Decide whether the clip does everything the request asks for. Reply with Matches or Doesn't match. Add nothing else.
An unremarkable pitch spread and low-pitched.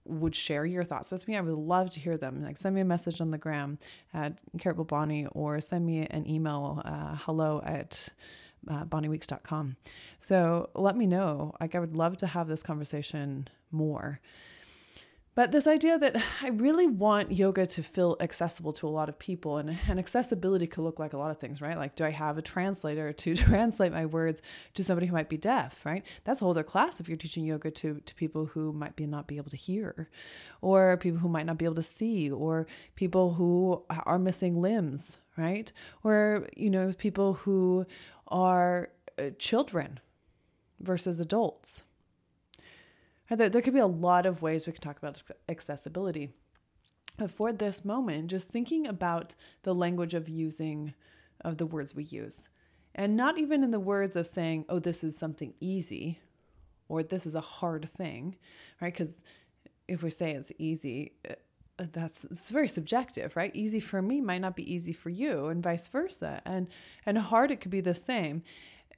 Doesn't match